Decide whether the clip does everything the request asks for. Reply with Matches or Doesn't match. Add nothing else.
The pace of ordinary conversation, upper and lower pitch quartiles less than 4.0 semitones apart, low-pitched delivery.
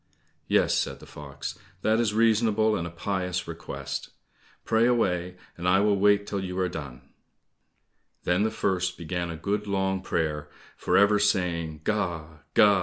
Matches